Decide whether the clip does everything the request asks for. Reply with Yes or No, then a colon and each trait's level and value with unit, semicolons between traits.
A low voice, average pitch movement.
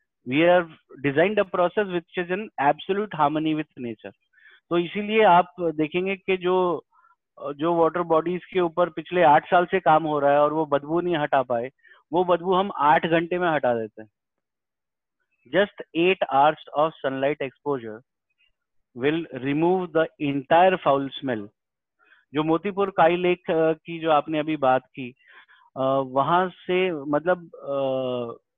No: medium, 160 Hz; average, 4.2 semitones